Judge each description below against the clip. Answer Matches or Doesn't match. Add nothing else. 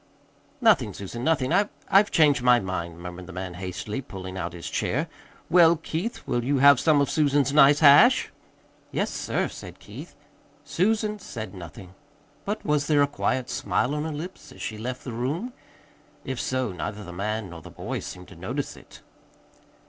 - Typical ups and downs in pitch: Doesn't match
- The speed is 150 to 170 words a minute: Doesn't match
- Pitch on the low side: Matches